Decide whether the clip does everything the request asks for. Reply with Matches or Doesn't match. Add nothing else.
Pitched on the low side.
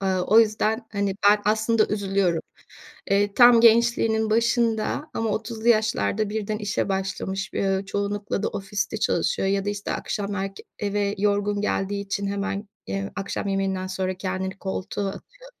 Doesn't match